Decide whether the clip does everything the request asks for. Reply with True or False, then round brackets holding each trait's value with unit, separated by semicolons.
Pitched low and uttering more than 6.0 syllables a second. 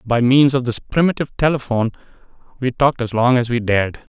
True (125 Hz; 6.4 syllables/s)